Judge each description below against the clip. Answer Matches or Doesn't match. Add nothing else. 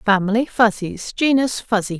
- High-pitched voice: Matches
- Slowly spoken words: Matches